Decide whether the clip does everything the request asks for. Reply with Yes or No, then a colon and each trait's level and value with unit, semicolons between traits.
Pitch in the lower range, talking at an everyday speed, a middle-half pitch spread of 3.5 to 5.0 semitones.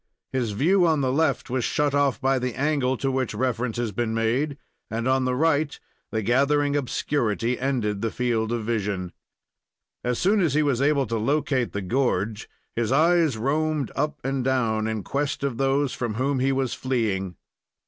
Yes: low, 130 Hz; average, 180 wpm; average, 3.8 semitones